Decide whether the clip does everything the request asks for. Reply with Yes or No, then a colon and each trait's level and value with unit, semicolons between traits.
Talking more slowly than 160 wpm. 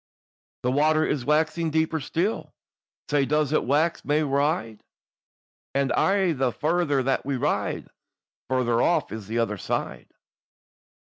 Yes: average, 140 wpm